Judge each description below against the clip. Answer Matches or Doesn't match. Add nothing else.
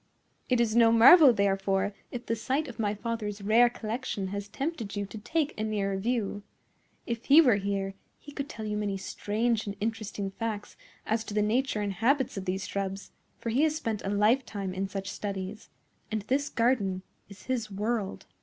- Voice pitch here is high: Matches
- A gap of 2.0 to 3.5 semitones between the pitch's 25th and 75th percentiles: Matches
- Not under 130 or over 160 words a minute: Doesn't match